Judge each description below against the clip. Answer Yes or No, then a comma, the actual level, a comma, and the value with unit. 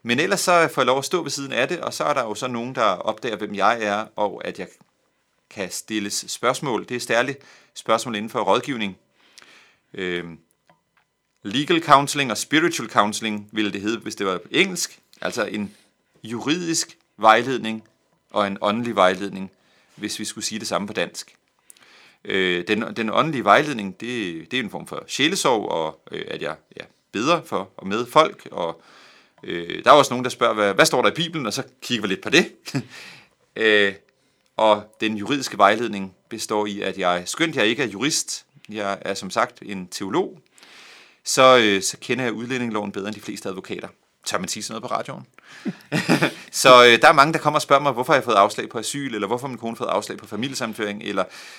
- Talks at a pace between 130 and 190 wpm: No, average, 200 wpm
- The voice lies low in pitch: Yes, low, 110 Hz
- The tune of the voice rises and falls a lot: No, average, 3.9 semitones